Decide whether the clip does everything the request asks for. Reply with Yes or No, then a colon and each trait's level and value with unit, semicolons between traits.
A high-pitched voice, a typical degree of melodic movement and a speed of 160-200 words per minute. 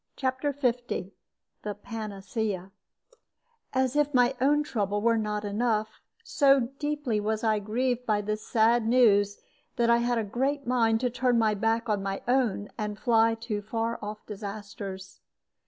No: high, 225 Hz; average, 3.0 semitones; average, 150 wpm